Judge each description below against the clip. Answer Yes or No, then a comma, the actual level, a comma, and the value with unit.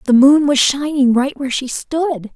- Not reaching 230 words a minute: Yes, fast, 205 wpm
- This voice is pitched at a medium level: No, very high, 275 Hz